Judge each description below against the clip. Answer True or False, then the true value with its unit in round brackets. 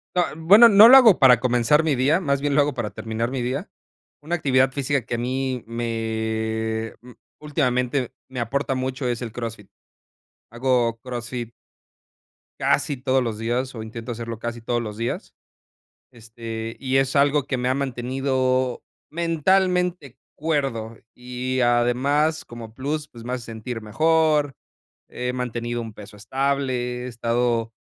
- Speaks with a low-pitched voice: True (125 Hz)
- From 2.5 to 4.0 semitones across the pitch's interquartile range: True (3.1 semitones)